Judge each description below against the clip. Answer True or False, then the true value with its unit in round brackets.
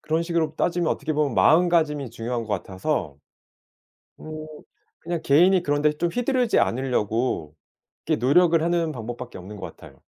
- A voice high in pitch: False (150 Hz)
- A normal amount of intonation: False (5.9 semitones)